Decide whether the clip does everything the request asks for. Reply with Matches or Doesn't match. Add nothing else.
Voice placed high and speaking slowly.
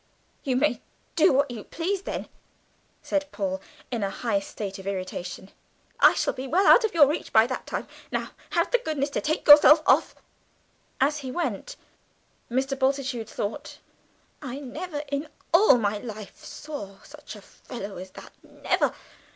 Doesn't match